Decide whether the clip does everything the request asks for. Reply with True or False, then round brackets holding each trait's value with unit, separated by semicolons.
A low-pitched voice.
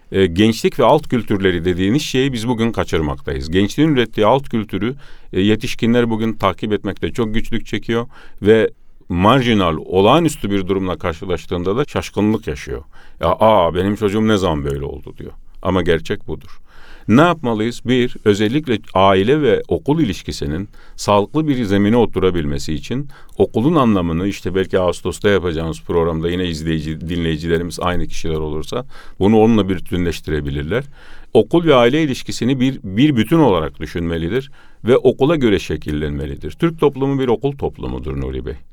True (100 Hz)